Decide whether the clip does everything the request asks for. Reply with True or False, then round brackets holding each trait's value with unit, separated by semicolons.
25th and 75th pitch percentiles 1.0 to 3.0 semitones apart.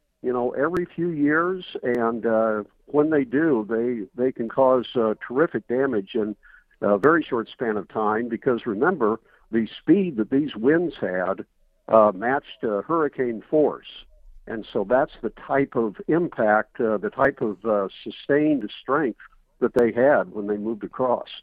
False (4.5 semitones)